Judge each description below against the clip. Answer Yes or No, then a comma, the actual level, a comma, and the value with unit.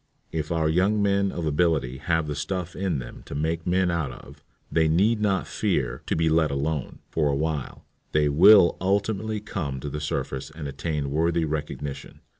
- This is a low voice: Yes, very low, 80 Hz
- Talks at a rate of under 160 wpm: No, average, 185 wpm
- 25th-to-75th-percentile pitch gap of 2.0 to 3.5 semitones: No, average, 4.0 semitones